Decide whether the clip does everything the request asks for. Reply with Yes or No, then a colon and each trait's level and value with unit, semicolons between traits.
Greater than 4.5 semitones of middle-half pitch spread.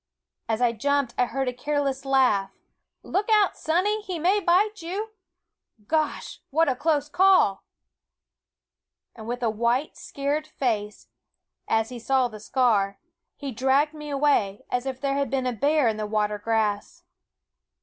Yes: average, 5.2 semitones